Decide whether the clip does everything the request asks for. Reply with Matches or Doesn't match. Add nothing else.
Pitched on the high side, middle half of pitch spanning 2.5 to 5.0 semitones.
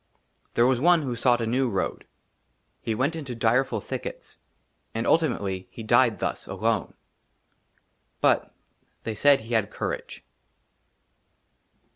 Doesn't match